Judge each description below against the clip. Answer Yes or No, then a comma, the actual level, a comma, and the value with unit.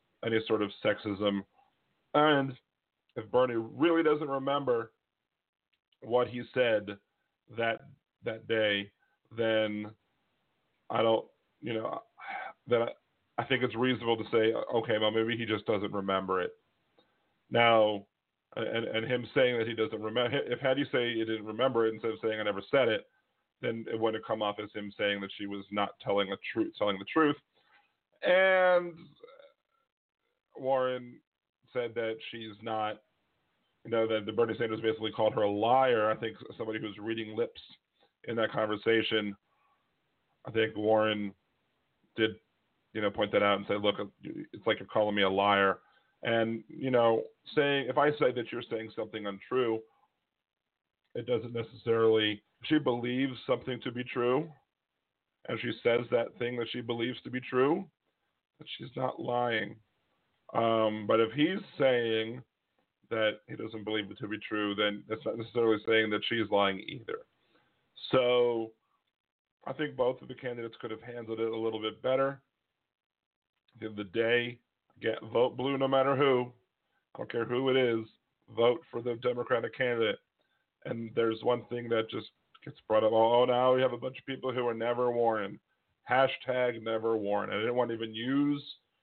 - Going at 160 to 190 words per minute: Yes, average, 165 wpm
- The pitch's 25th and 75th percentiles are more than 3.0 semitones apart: No, average, 2.7 semitones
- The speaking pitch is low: Yes, low, 115 Hz